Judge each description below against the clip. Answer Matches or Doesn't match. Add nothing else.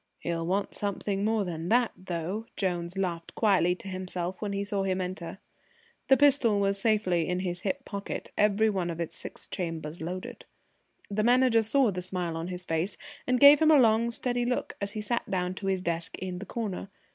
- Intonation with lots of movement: Doesn't match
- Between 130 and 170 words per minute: Doesn't match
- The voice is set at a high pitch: Matches